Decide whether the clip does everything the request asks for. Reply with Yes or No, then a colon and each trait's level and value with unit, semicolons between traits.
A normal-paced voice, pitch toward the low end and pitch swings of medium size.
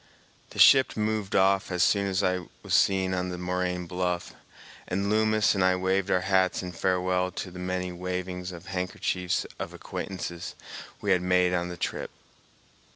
No: average, 170 wpm; very low, 90 Hz; narrow, 1.0 semitones